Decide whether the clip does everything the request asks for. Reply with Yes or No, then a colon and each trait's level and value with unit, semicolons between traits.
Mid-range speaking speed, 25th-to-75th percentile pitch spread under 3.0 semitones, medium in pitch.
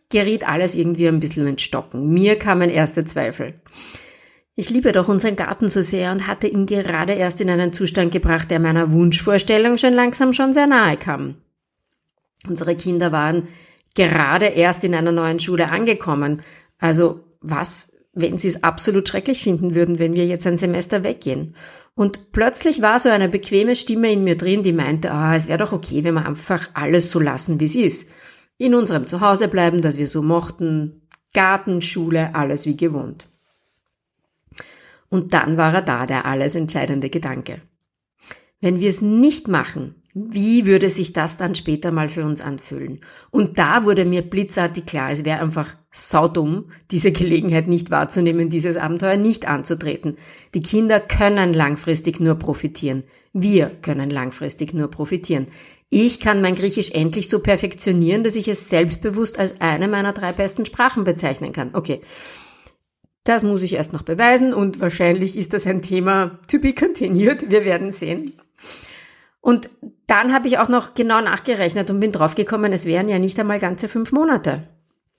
No: average, 170 wpm; average, 4.1 semitones; medium, 180 Hz